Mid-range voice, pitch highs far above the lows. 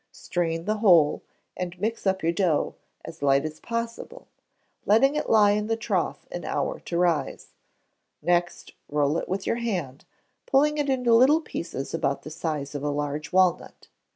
Yes: medium, 180 Hz; wide, 7.1 semitones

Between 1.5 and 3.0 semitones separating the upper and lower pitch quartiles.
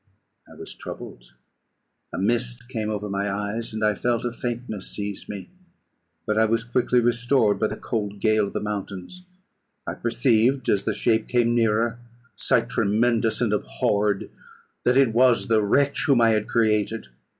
Yes: narrow, 2.4 semitones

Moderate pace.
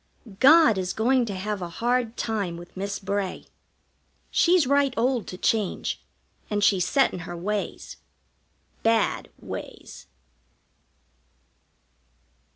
No: slow, 115 wpm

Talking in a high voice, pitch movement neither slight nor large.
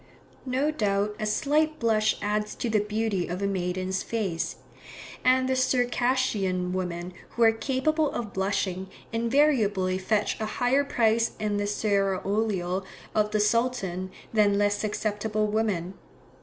Yes: high, 210 Hz; average, 3.4 semitones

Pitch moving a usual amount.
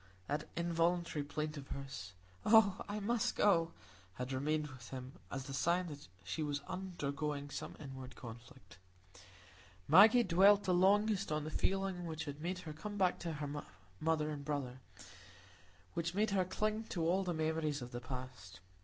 Yes: average, 4.8 semitones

